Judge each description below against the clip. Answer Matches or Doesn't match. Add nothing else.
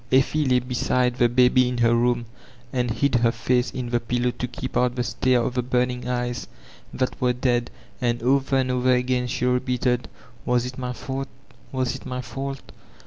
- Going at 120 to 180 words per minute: Doesn't match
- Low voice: Matches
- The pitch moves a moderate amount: Doesn't match